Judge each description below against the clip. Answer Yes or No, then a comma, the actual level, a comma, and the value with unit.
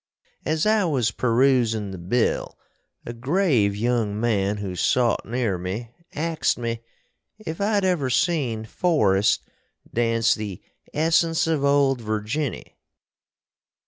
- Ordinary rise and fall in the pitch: No, wide, 6.2 semitones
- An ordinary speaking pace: No, slow, 115 wpm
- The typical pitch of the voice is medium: No, low, 120 Hz